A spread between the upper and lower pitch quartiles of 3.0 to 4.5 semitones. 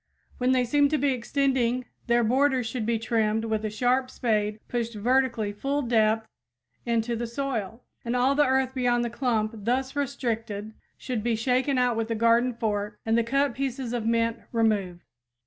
No: narrow, 2.5 semitones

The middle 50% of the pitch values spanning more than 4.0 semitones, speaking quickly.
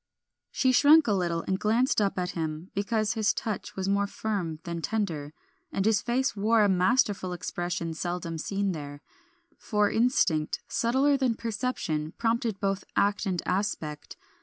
No: average, 4.5 semitones; average, 155 wpm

